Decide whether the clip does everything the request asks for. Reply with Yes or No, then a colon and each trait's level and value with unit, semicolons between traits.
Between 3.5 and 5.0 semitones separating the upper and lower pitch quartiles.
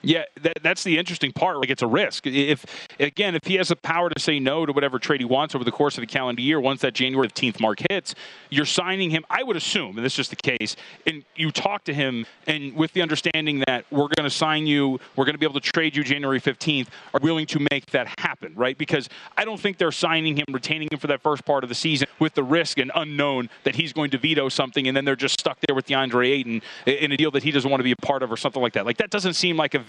No: average, 2.8 semitones